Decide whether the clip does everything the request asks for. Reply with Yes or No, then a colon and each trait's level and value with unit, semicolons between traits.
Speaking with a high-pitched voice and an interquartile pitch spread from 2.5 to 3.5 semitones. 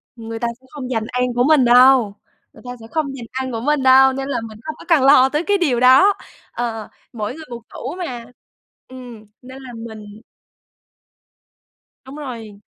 Yes: very high, 255 Hz; average, 2.8 semitones